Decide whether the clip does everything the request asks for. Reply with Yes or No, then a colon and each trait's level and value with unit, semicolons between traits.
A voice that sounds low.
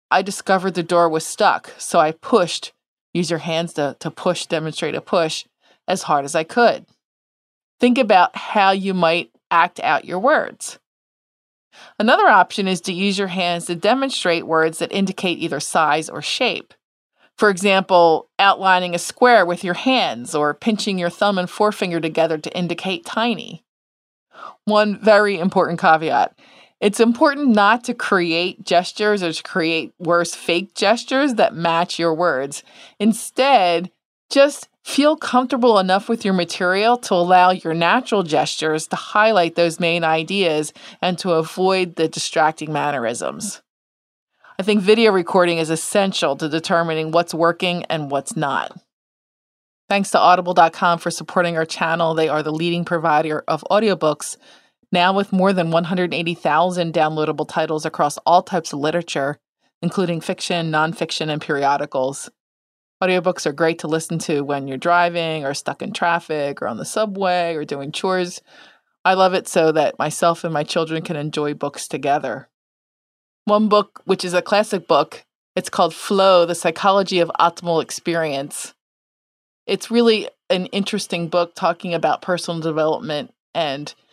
No: medium, 175 Hz